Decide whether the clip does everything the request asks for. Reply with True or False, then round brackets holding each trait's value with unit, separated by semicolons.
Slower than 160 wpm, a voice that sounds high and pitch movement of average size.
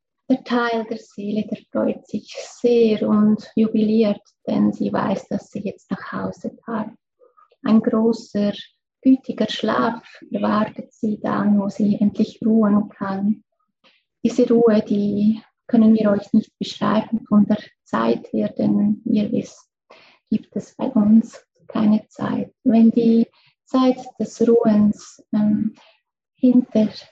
False (130 wpm; 225 Hz; 2.1 semitones)